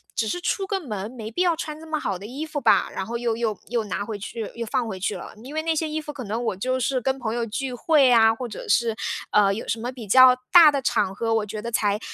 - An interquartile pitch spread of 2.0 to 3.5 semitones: No, average, 4.6 semitones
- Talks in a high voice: Yes, high, 240 Hz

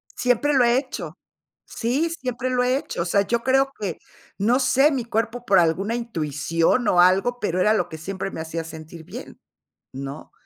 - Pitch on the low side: No, high, 220 Hz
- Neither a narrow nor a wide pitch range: No, wide, 6.9 semitones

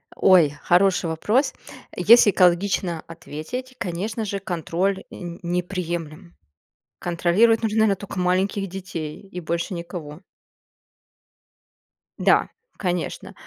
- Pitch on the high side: No, medium, 180 Hz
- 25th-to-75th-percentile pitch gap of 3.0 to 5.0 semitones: No, narrow, 2.6 semitones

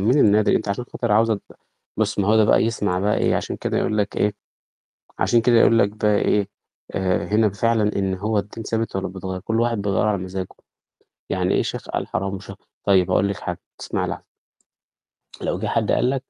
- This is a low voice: Yes, low, 105 Hz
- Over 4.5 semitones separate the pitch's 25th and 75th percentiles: No, narrow, 2.5 semitones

